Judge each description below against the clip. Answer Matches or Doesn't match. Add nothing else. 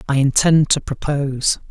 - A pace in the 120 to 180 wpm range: Matches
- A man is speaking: Matches